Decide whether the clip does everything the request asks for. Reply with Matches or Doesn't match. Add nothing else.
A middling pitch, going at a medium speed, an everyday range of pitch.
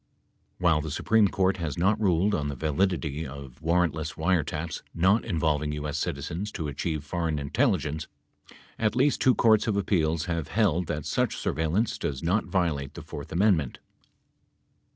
Doesn't match